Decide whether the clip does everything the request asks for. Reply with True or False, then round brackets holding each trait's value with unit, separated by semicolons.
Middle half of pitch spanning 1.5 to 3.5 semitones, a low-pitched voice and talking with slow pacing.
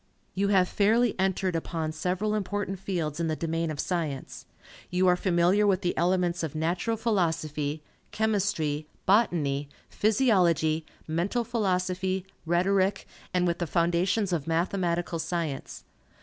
False (3.1 semitones; 180 Hz; 130 wpm)